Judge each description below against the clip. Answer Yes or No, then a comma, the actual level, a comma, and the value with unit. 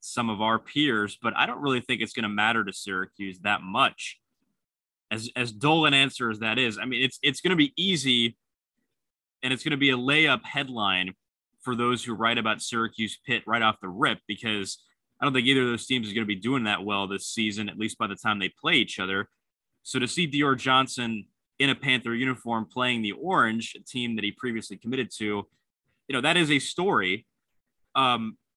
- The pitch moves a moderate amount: Yes, average, 3.3 semitones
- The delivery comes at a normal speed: No, fast, 220 wpm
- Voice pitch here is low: Yes, low, 120 Hz